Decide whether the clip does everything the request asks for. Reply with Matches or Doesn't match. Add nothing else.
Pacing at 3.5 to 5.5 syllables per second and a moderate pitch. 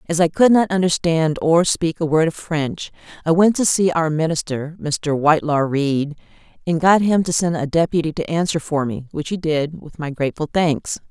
Matches